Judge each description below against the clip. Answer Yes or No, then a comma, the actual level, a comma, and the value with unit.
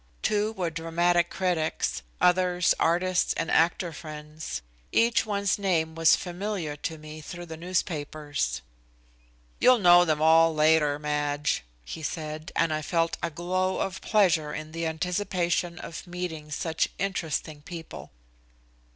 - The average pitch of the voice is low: No, medium, 165 Hz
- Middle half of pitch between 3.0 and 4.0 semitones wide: No, narrow, 2.6 semitones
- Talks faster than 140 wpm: No, slow, 135 wpm